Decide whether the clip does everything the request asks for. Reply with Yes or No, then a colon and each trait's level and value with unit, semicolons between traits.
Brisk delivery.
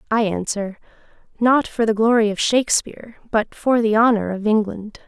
No: average, 165 wpm